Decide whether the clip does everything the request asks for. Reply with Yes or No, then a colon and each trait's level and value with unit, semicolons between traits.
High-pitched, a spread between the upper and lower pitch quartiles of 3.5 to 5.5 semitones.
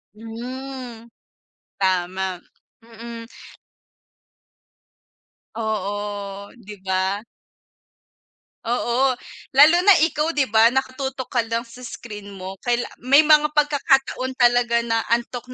Yes: high, 235 Hz; average, 4.0 semitones